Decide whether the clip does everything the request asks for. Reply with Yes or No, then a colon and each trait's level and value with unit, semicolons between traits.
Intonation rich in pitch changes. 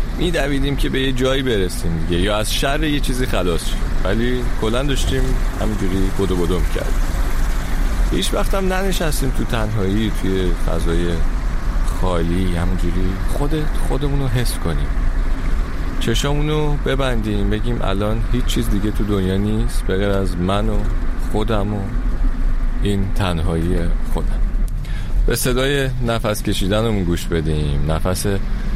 Yes: wide, 5.8 semitones